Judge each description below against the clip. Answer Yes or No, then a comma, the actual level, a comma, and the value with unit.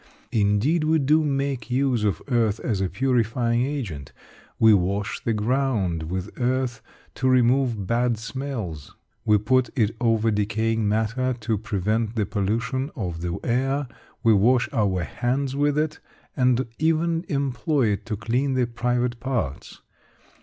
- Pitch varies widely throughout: No, average, 3.8 semitones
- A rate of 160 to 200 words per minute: No, average, 145 wpm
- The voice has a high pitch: No, low, 120 Hz